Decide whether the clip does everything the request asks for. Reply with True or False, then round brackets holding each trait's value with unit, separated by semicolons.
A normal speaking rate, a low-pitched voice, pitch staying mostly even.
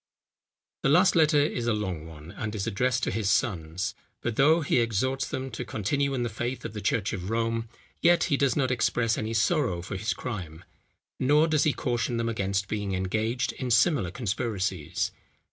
False (190 wpm; 115 Hz; 4.8 semitones)